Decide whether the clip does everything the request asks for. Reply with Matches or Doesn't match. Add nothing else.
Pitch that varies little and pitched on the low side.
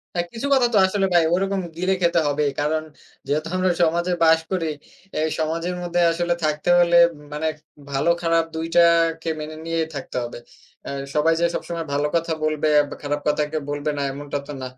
Doesn't match